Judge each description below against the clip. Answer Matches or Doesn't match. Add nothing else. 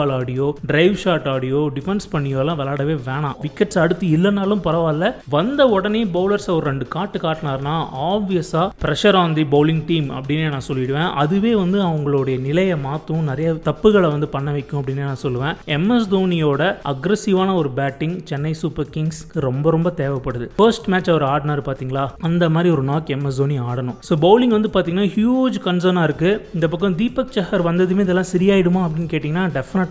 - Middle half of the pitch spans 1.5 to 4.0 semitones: Doesn't match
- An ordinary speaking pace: Doesn't match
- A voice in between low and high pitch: Matches